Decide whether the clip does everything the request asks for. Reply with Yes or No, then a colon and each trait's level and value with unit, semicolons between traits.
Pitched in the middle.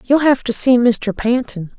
No: high, 240 Hz